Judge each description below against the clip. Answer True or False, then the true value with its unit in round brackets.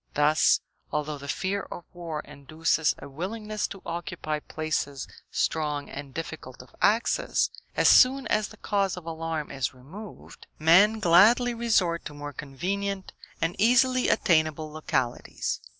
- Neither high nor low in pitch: True (165 Hz)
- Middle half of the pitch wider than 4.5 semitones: True (5.2 semitones)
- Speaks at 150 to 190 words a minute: False (135 wpm)